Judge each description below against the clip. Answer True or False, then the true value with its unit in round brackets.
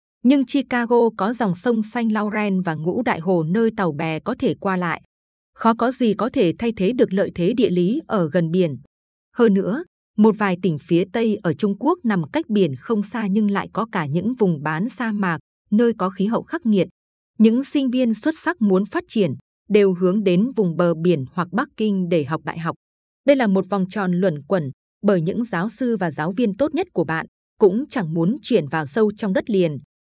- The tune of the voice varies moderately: True (4.6 semitones)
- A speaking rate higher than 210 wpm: True (220 wpm)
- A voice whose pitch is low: False (205 Hz)